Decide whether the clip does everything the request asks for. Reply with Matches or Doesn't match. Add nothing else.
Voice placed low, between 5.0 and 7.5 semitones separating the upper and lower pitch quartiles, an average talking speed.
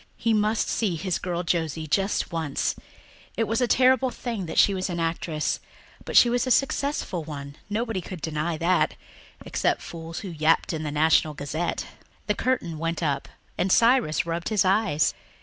Doesn't match